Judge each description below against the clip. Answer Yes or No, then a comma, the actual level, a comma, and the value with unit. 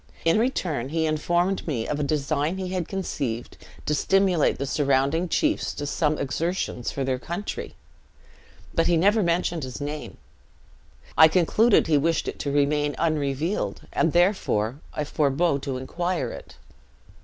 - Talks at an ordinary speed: Yes, average, 155 wpm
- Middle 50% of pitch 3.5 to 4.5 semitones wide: Yes, average, 3.8 semitones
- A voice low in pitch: No, medium, 155 Hz